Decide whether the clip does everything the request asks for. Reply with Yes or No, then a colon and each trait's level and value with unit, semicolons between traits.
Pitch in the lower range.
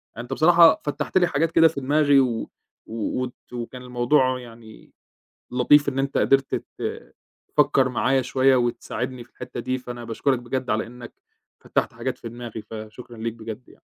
Yes: low, 125 Hz